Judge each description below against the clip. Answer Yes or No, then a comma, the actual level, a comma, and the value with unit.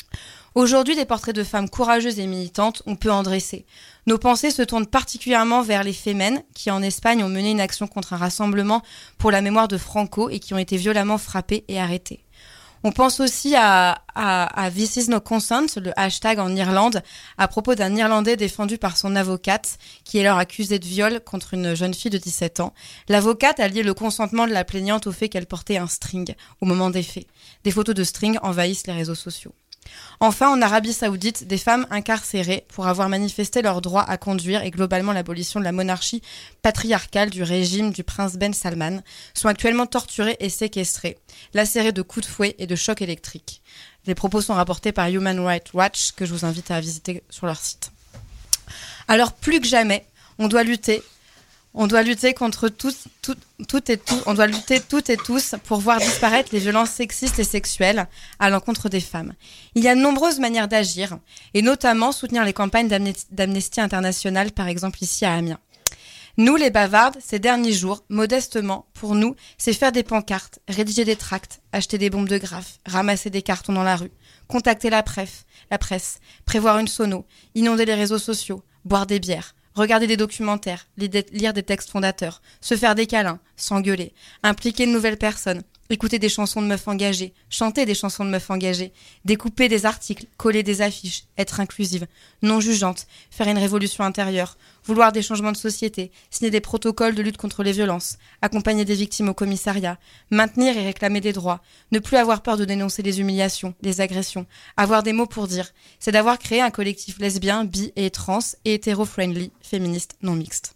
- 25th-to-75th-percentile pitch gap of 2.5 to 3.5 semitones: Yes, average, 2.8 semitones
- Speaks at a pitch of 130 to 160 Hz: No, high, 205 Hz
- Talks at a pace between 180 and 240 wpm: Yes, average, 190 wpm